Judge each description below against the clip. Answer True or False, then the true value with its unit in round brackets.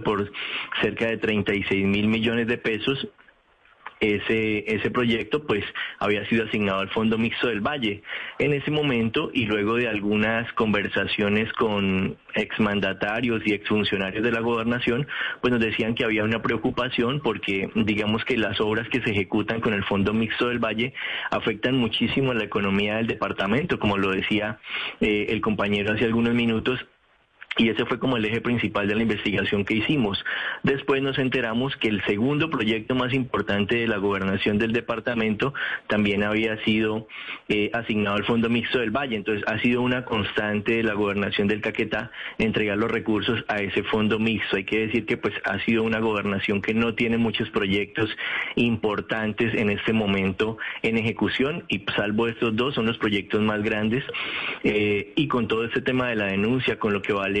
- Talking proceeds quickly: False (175 wpm)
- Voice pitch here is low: True (110 Hz)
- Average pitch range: False (2.1 semitones)